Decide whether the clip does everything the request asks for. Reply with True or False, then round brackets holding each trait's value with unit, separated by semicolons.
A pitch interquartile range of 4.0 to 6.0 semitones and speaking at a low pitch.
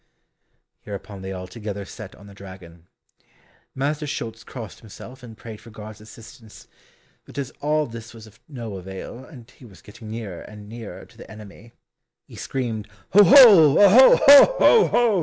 True (4.8 semitones; 115 Hz)